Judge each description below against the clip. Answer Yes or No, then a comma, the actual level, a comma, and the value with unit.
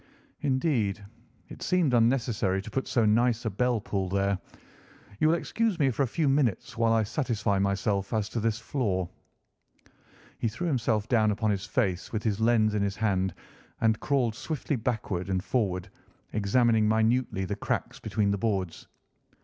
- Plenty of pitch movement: No, average, 3.7 semitones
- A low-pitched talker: Yes, low, 110 Hz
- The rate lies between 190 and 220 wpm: No, average, 165 wpm